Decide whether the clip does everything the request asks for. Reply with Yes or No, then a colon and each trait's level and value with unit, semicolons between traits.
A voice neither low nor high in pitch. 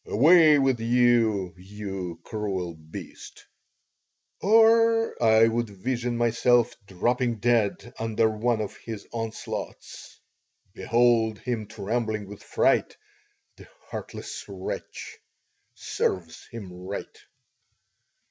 No: low, 115 Hz